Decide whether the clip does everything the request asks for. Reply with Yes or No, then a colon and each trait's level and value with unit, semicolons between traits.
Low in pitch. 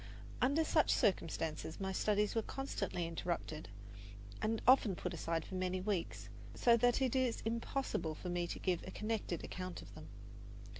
No: high, 195 Hz